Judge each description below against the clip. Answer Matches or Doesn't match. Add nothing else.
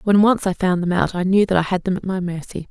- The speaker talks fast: Matches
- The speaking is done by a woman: Matches